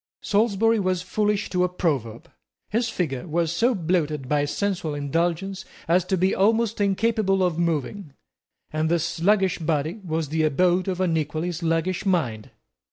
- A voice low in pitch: No, medium, 175 Hz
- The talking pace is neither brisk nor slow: Yes, average, 155 wpm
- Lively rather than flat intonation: No, average, 3.5 semitones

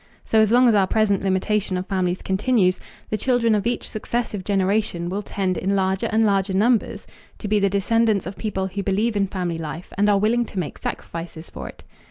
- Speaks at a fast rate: Yes, fast, 210 wpm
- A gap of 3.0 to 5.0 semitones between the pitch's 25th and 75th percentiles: No, narrow, 2.5 semitones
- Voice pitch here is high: Yes, high, 200 Hz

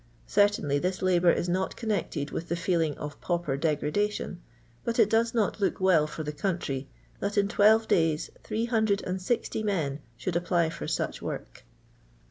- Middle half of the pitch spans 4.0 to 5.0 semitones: Yes, average, 4.4 semitones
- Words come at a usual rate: Yes, average, 155 wpm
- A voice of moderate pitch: Yes, medium, 180 Hz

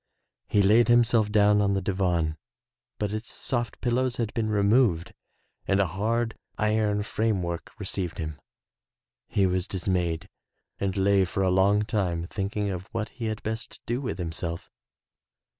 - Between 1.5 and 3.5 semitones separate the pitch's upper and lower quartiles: Yes, average, 3.0 semitones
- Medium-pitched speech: No, low, 100 Hz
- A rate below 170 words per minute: Yes, average, 160 wpm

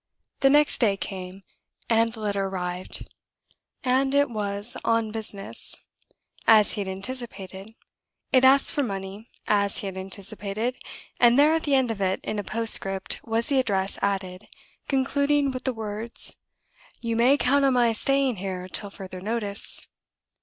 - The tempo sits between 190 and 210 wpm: No, average, 155 wpm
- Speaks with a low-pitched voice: No, high, 220 Hz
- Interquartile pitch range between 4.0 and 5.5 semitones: Yes, average, 4.6 semitones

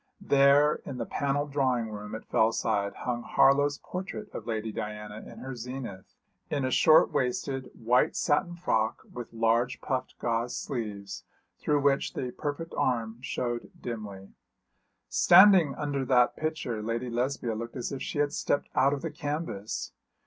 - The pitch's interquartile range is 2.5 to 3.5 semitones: No, average, 4.0 semitones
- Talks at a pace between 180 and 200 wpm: No, average, 155 wpm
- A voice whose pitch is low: Yes, low, 125 Hz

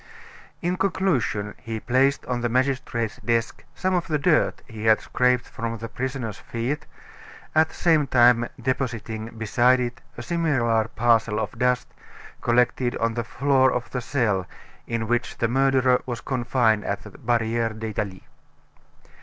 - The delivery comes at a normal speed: Yes, average, 150 wpm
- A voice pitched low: Yes, low, 120 Hz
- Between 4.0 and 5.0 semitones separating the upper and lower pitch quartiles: No, narrow, 2.6 semitones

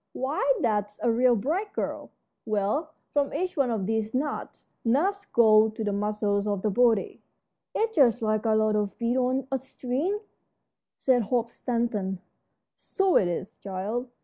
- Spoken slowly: No, average, 160 wpm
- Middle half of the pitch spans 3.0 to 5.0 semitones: Yes, average, 4.0 semitones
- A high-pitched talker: Yes, high, 230 Hz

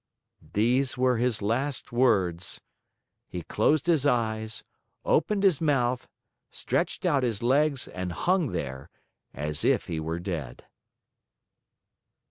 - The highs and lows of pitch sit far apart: Yes, wide, 7.2 semitones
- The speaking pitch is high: No, low, 120 Hz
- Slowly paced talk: Yes, slow, 115 wpm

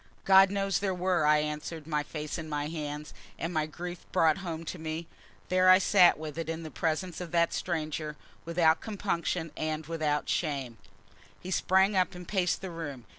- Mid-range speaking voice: Yes, medium, 165 Hz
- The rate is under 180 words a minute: No, average, 185 wpm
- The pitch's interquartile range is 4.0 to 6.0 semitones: No, average, 2.9 semitones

